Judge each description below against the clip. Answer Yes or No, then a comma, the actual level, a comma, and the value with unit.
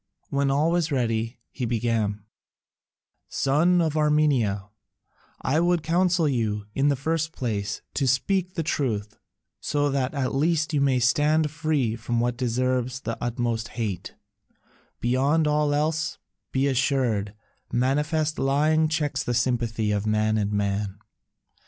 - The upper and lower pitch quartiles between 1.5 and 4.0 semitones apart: No, average, 4.8 semitones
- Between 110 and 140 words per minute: Yes, slow, 135 wpm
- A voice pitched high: No, low, 135 Hz